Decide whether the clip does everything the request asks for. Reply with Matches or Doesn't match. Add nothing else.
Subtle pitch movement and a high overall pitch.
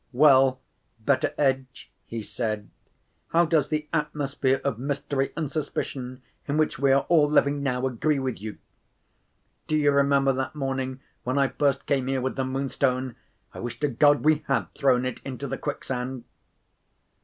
Doesn't match